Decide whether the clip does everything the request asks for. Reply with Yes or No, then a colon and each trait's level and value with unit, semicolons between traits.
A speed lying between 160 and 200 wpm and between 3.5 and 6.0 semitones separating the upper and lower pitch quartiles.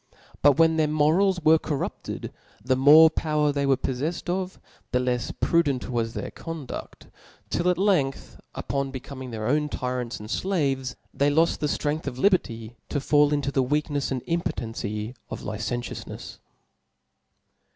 No: average, 150 wpm; average, 4.0 semitones